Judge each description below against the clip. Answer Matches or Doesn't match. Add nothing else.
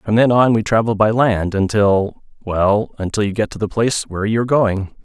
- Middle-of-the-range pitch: Doesn't match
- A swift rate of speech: Matches